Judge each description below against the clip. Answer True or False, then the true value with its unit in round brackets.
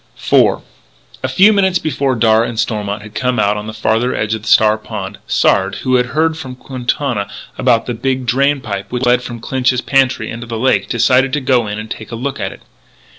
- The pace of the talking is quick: True (215 wpm)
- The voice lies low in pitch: True (120 Hz)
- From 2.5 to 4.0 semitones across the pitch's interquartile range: True (3.2 semitones)